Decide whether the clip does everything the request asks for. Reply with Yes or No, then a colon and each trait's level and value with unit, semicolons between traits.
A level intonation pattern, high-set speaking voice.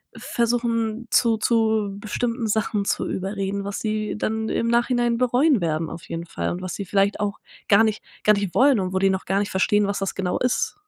No: average, 3.0 semitones; high, 210 Hz